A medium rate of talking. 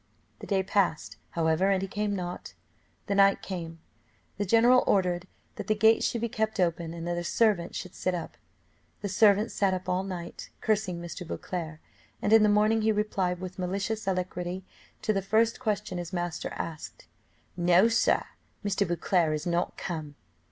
Yes: average, 175 wpm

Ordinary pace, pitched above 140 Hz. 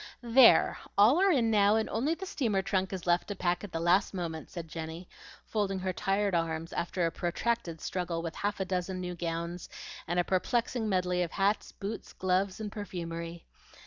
Yes: average, 190 wpm; medium, 185 Hz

